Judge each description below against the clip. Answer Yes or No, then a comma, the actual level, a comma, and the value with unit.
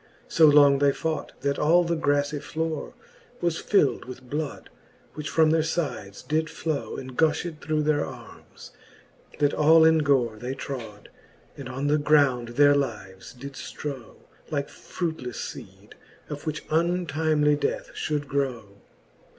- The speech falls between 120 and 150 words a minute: Yes, average, 145 wpm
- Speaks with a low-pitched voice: No, medium, 145 Hz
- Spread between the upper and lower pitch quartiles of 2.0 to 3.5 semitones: Yes, average, 2.8 semitones